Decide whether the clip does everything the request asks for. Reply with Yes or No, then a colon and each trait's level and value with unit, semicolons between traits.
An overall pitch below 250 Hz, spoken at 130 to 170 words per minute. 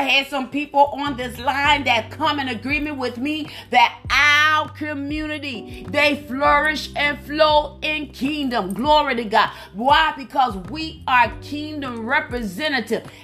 No: very high, 285 Hz; average, 140 wpm